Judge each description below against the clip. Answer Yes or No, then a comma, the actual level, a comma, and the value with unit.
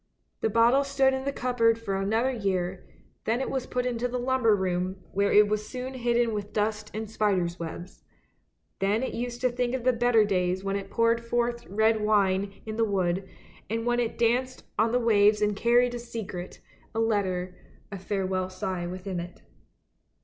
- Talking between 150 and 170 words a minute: No, average, 185 wpm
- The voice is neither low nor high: No, high, 220 Hz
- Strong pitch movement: No, average, 3.8 semitones